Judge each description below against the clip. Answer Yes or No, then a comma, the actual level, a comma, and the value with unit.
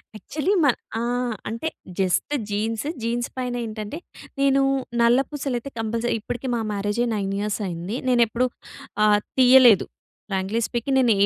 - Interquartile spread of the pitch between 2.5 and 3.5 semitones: Yes, average, 3.2 semitones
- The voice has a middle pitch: No, high, 235 Hz